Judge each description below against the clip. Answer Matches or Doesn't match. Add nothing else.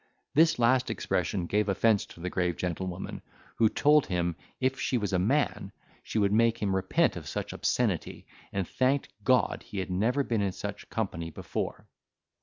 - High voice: Doesn't match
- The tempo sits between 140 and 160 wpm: Doesn't match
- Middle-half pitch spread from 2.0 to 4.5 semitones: Doesn't match